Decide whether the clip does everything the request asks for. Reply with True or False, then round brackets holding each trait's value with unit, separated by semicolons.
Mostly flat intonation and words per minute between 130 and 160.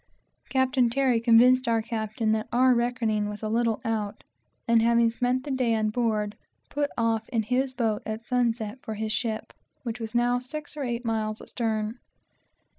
False (2.2 semitones; 175 wpm)